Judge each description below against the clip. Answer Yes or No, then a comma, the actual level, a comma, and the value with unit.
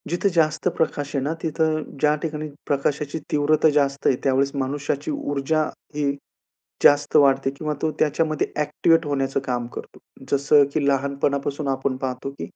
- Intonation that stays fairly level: Yes, narrow, 1.9 semitones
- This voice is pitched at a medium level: Yes, medium, 145 Hz